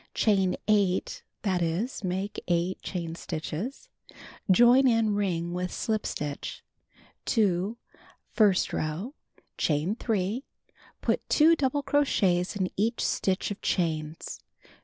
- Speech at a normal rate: No, slow, 115 wpm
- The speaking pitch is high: Yes, high, 195 Hz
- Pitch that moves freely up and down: No, average, 4.5 semitones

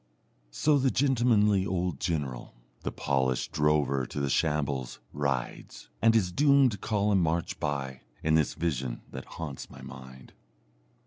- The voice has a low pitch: Yes, very low, 75 Hz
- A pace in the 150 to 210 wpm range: No, slow, 135 wpm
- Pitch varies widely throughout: Yes, wide, 7.3 semitones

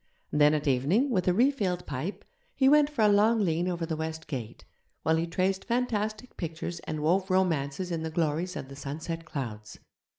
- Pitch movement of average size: Yes, average, 4.8 semitones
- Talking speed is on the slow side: No, average, 190 wpm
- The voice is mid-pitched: Yes, medium, 170 Hz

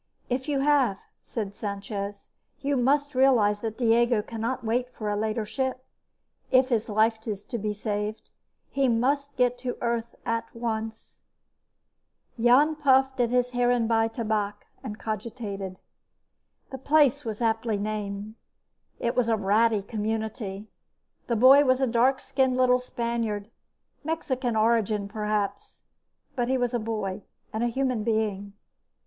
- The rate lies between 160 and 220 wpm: No, average, 140 wpm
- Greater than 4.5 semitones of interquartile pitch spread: No, average, 3.0 semitones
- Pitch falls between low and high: No, high, 230 Hz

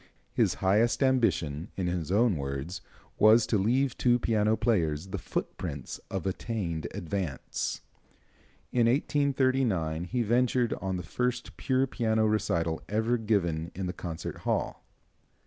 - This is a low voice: Yes, low, 105 Hz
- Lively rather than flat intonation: Yes, wide, 5.9 semitones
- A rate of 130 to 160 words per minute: Yes, slow, 135 wpm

